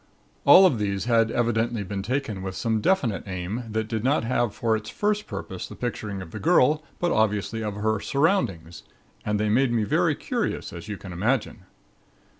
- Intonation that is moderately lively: Yes, average, 3.7 semitones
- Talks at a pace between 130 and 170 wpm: No, average, 190 wpm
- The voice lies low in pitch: Yes, low, 110 Hz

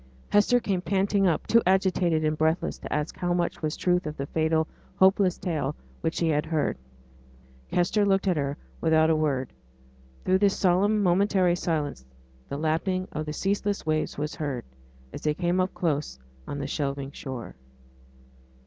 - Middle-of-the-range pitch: Yes, medium, 165 Hz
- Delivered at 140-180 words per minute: Yes, average, 165 wpm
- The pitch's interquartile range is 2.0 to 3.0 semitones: No, average, 3.8 semitones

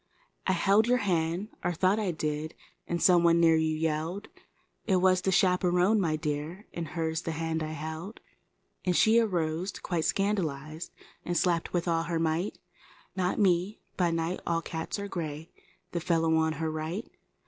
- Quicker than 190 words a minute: No, average, 160 wpm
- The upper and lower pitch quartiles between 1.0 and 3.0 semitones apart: Yes, narrow, 2.6 semitones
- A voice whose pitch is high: No, medium, 170 Hz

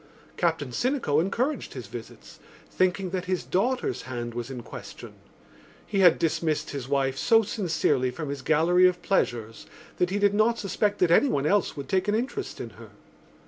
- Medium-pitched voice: Yes, medium, 180 Hz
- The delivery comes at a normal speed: Yes, average, 175 wpm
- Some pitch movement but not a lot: No, wide, 6.4 semitones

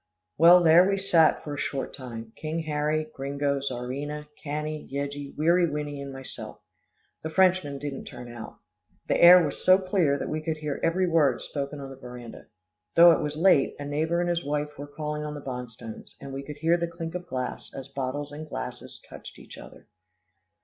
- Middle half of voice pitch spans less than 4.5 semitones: Yes, average, 3.0 semitones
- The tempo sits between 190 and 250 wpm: Yes, average, 195 wpm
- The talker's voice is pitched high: No, medium, 150 Hz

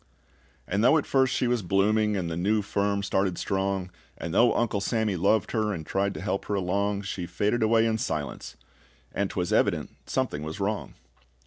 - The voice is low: Yes, low, 100 Hz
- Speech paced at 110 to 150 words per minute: No, average, 190 wpm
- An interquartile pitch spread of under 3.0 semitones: Yes, narrow, 2.6 semitones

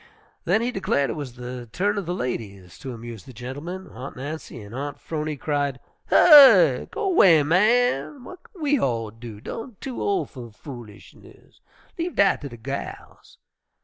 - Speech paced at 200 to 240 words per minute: No, average, 170 wpm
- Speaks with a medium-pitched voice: Yes, medium, 145 Hz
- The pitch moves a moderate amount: No, wide, 8.9 semitones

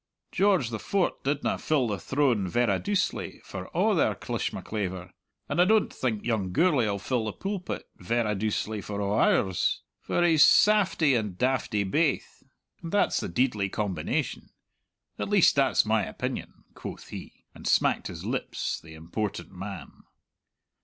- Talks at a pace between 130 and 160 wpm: Yes, average, 150 wpm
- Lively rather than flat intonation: Yes, wide, 7.4 semitones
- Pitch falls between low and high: No, low, 115 Hz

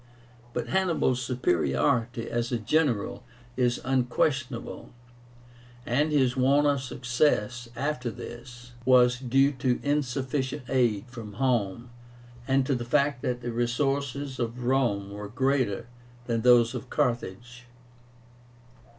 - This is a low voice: Yes, low, 125 Hz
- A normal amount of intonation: No, narrow, 2.1 semitones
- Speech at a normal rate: No, slow, 115 wpm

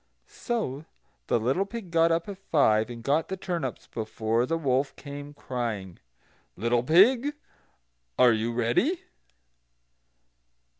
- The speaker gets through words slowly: Yes, slow, 120 wpm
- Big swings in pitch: Yes, wide, 6.7 semitones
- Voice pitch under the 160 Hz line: Yes, medium, 140 Hz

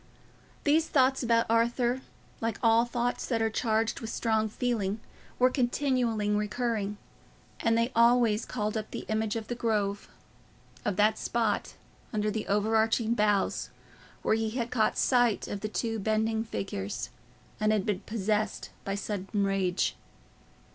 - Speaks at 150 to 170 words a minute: No, average, 140 wpm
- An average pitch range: No, narrow, 2.1 semitones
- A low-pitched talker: No, high, 220 Hz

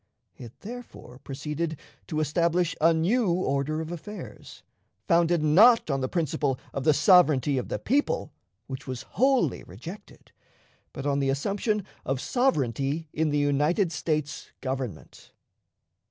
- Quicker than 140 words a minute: No, slow, 135 wpm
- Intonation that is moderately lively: Yes, average, 4.1 semitones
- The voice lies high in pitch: No, medium, 155 Hz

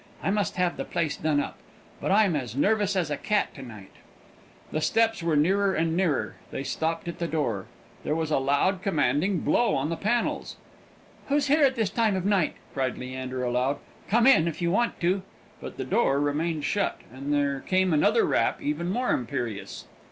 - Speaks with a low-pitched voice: No, medium, 165 Hz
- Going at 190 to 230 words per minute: Yes, average, 195 wpm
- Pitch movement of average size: No, wide, 5.8 semitones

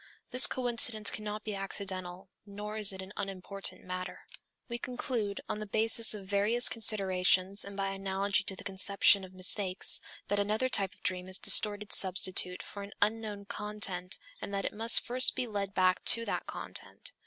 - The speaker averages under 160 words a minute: No, average, 175 wpm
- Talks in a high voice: Yes, high, 200 Hz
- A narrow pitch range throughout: Yes, narrow, 2.0 semitones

